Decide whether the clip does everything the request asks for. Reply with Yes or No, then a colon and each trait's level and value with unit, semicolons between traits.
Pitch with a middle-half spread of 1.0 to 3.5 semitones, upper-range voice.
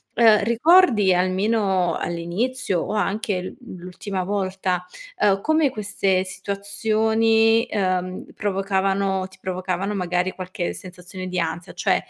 Yes: average, 2.7 semitones; high, 195 Hz